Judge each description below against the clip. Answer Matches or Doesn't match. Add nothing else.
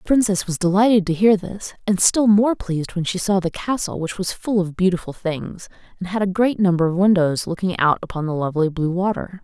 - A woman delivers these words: Matches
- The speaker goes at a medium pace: Doesn't match